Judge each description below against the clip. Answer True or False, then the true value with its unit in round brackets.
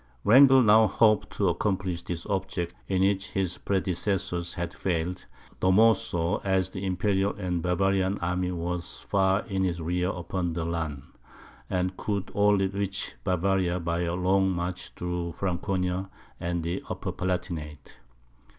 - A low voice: True (90 Hz)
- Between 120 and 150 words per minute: True (145 wpm)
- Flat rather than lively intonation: True (2.0 semitones)